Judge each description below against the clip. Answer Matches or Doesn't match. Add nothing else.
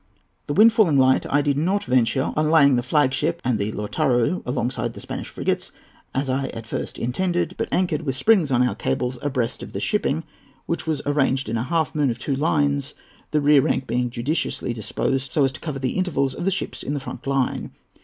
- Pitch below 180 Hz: Matches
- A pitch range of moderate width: Matches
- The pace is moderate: Doesn't match